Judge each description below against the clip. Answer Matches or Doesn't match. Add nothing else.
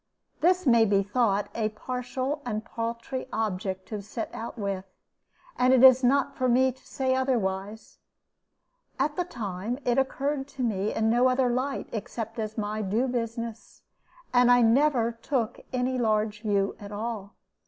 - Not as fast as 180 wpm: Matches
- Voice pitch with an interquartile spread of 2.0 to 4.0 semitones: Matches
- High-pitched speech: Matches